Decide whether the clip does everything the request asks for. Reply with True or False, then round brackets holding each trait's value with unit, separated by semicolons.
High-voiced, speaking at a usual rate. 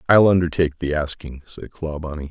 False (80 Hz; 155 wpm)